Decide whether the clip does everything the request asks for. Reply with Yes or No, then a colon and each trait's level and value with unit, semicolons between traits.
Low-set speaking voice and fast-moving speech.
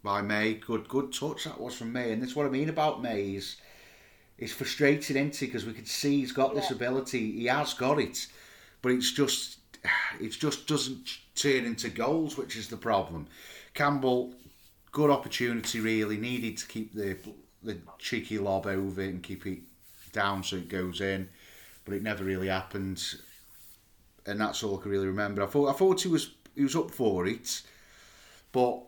No: low, 110 Hz; average, 185 wpm